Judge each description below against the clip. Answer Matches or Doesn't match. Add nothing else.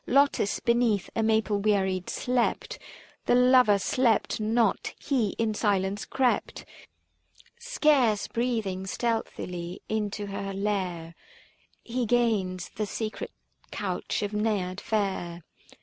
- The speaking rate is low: Matches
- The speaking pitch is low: Doesn't match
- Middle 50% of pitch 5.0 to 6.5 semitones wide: Doesn't match